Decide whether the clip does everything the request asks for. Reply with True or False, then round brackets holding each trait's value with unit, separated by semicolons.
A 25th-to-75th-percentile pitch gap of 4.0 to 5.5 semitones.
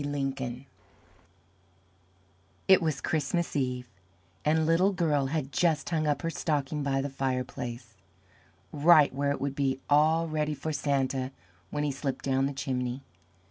False (2.7 semitones)